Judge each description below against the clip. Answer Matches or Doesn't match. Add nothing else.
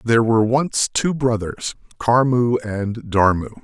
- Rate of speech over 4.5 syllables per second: Doesn't match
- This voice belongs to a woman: Doesn't match